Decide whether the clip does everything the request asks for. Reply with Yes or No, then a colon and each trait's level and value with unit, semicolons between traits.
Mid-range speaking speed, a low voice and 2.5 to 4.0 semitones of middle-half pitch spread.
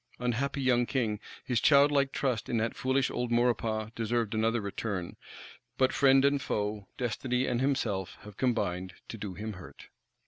Yes: average, 160 wpm; low, 120 Hz; average, 3.5 semitones